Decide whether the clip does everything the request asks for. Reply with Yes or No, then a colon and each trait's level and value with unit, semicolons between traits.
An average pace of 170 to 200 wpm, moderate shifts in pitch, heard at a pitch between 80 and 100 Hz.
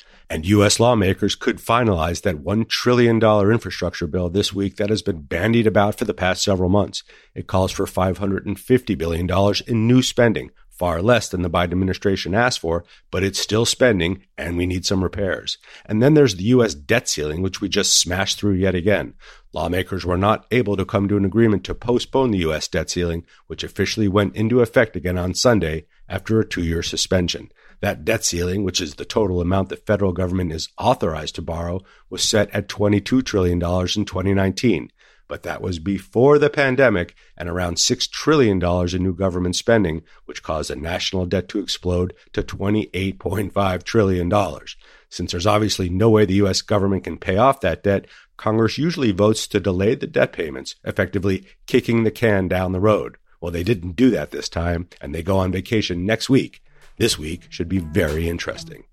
Yes: average, 185 wpm; average, 3.1 semitones; very low, 95 Hz